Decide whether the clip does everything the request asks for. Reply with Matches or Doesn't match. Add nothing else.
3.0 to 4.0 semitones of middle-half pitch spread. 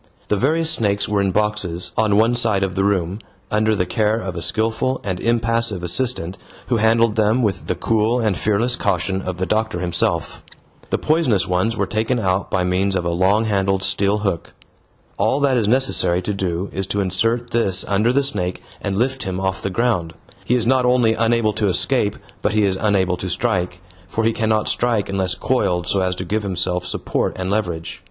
Matches